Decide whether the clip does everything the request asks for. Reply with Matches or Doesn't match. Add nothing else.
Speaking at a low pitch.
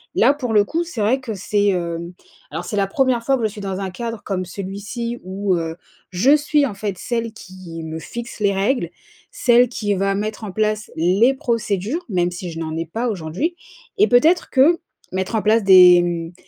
Doesn't match